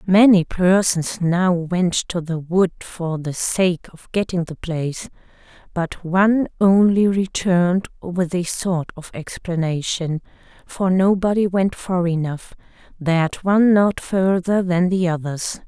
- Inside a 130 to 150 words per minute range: Yes, slow, 135 wpm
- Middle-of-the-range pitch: Yes, medium, 180 Hz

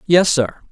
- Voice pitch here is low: No, medium, 155 Hz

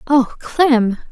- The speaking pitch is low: No, very high, 255 Hz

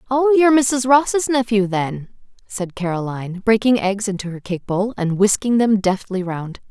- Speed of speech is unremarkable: Yes, average, 170 wpm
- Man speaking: No, female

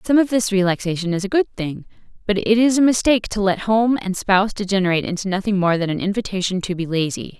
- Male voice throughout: No, female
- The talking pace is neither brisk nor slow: No, fast, 225 wpm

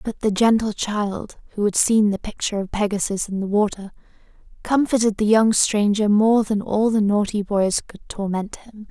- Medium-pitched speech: No, high, 210 Hz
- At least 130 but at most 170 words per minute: No, average, 180 wpm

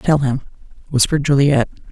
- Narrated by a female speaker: Yes, female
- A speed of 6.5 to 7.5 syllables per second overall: Yes, 6.7 syllables/s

